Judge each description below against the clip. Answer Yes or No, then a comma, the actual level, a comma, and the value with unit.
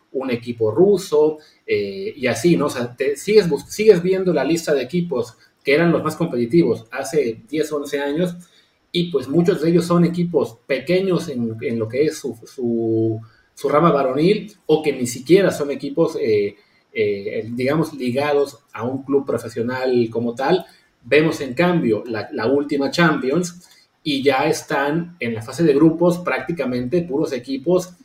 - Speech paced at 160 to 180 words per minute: Yes, average, 170 wpm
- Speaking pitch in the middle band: Yes, medium, 155 Hz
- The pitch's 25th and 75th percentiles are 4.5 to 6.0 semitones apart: Yes, average, 5.2 semitones